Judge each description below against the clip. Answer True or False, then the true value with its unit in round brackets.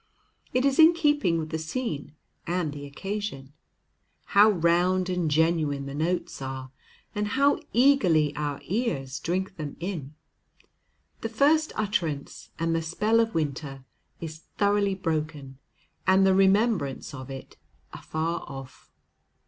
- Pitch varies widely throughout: True (5.9 semitones)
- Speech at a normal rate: False (130 wpm)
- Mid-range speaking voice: True (170 Hz)